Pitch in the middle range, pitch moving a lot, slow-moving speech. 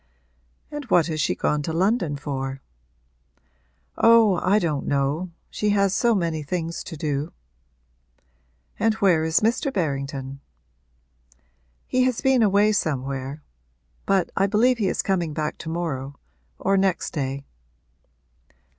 Yes: medium, 170 Hz; wide, 6.2 semitones; slow, 130 wpm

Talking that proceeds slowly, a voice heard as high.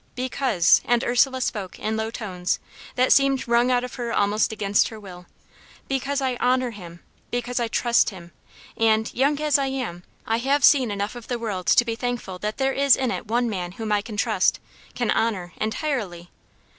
No: average, 195 wpm; high, 235 Hz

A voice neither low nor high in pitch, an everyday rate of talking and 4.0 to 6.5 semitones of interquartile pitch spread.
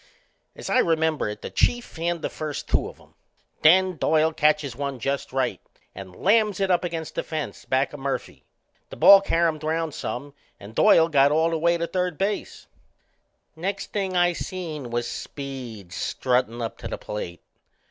Yes: medium, 155 Hz; average, 180 wpm; average, 4.5 semitones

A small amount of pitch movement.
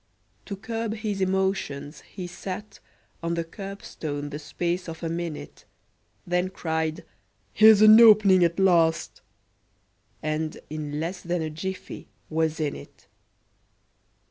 No: average, 3.4 semitones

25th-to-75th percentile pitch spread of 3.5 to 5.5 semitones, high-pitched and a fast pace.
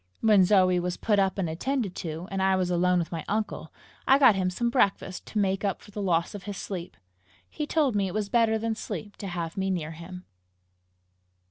No: average, 3.0 semitones; high, 195 Hz; fast, 220 wpm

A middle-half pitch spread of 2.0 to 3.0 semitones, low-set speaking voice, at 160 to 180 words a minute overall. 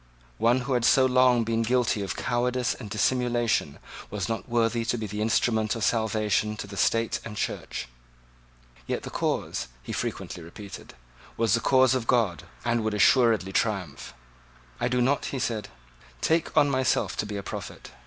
Yes: average, 2.7 semitones; low, 115 Hz; average, 175 wpm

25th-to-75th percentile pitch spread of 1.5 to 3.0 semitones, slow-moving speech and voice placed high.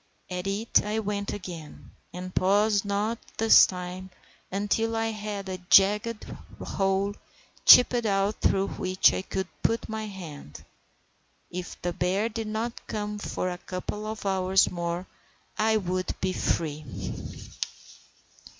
Yes: average, 2.7 semitones; slow, 130 wpm; high, 195 Hz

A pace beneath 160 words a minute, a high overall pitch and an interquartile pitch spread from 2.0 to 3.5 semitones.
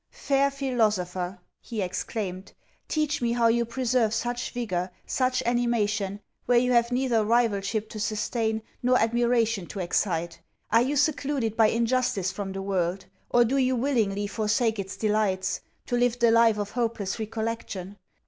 Yes: average, 150 wpm; high, 225 Hz; average, 3.1 semitones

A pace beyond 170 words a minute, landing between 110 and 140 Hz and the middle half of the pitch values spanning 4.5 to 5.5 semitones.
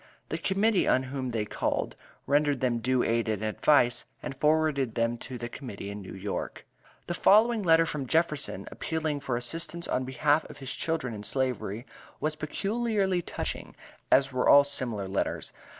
No: average, 165 wpm; low, 135 Hz; average, 5.1 semitones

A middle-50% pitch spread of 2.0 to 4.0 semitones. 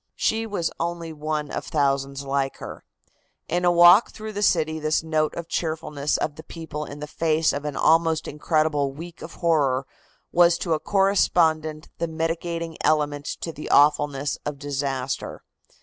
Yes: narrow, 2.4 semitones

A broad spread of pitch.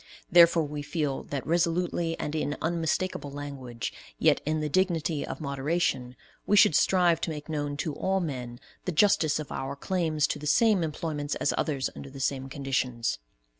No: average, 3.3 semitones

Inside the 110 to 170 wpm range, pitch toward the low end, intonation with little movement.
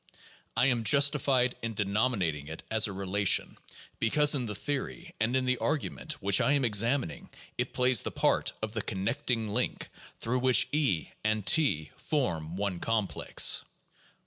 No: average, 165 wpm; low, 115 Hz; average, 4.6 semitones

